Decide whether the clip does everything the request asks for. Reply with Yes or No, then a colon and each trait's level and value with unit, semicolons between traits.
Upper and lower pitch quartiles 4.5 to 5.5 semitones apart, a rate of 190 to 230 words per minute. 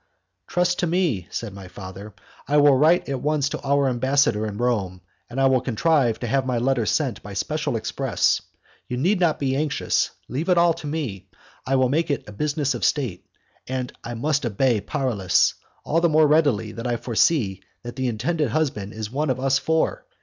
Yes: average, 4.9 semitones; average, 200 wpm